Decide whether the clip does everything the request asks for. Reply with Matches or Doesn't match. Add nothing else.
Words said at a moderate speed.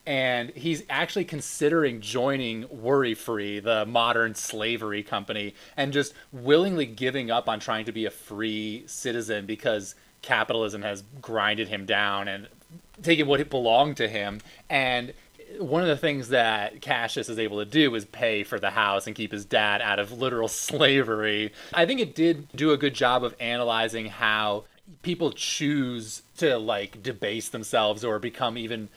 Matches